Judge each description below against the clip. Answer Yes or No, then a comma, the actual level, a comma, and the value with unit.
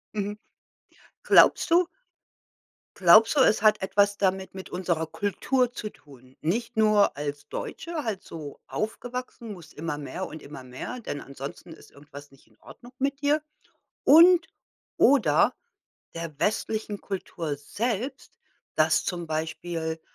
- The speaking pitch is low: No, high, 190 Hz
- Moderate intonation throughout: No, wide, 6.9 semitones